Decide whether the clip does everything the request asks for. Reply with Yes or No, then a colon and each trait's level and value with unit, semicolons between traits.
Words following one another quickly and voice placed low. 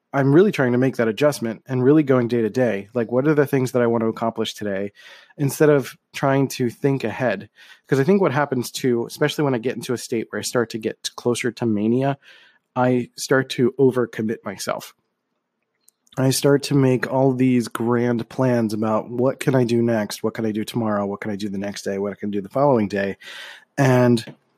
Yes: fast, 220 wpm; low, 125 Hz